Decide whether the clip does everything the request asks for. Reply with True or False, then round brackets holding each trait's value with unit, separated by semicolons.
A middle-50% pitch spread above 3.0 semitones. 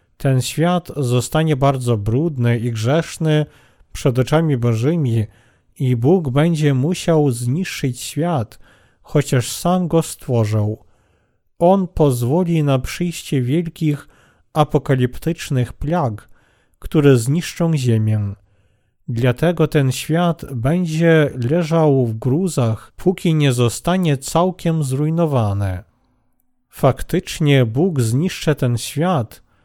True (5.1 semitones)